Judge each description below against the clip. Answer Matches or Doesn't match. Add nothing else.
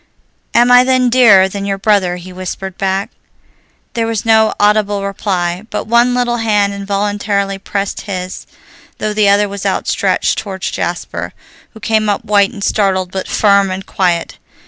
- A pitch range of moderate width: Doesn't match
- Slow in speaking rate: Doesn't match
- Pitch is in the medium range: Doesn't match